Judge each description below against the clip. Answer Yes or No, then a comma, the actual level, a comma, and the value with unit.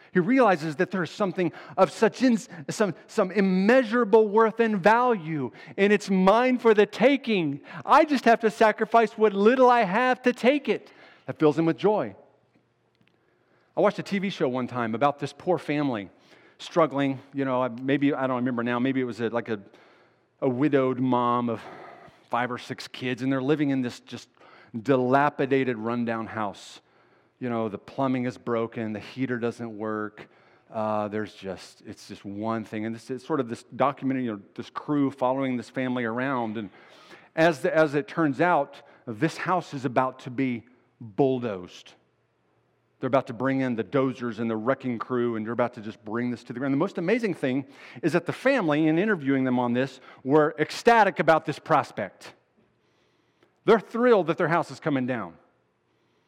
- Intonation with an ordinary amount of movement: No, wide, 7.1 semitones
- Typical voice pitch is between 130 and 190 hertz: Yes, medium, 140 Hz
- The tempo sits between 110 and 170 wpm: No, average, 185 wpm